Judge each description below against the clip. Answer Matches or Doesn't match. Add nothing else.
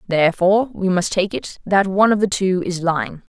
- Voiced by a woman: Matches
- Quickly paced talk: Matches